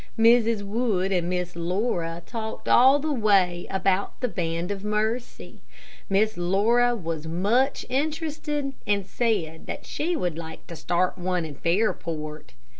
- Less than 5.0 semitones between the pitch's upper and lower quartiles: No, average, 5.3 semitones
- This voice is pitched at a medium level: No, high, 200 Hz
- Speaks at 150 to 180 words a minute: No, average, 140 wpm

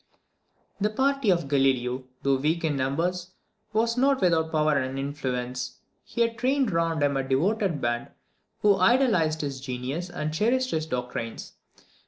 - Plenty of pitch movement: Yes, wide, 7.5 semitones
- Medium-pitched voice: Yes, medium, 160 Hz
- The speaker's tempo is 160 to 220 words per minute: No, average, 150 wpm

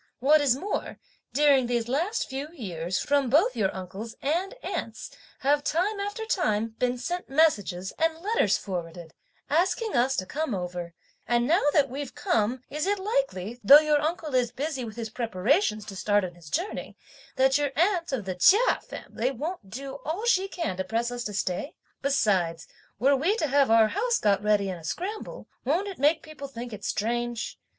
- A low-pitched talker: No, very high, 265 Hz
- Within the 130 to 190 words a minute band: Yes, average, 185 wpm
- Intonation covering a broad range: Yes, wide, 7.1 semitones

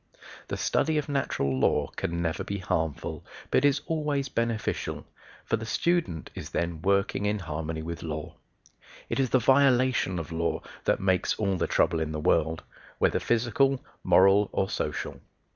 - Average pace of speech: Yes, average, 160 wpm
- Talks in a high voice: No, low, 100 Hz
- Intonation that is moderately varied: No, wide, 8.0 semitones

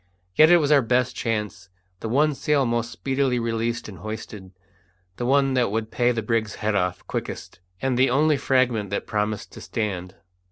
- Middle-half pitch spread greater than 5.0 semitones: No, average, 3.7 semitones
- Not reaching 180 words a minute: No, average, 185 wpm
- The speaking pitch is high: No, low, 115 Hz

